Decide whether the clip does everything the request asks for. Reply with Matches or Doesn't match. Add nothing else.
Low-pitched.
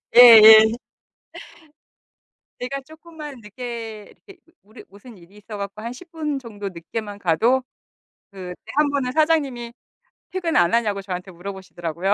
Doesn't match